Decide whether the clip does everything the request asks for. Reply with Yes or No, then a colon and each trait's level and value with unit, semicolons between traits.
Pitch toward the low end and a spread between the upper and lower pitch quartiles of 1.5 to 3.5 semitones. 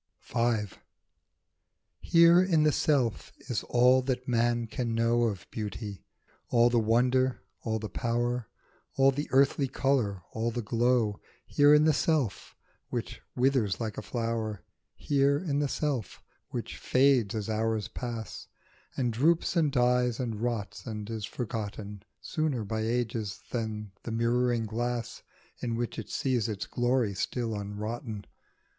Yes: low, 120 Hz; average, 2.8 semitones